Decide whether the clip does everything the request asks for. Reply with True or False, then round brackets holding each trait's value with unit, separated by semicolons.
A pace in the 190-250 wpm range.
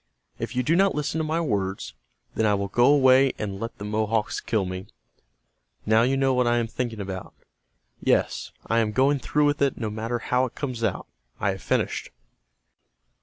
True (195 wpm)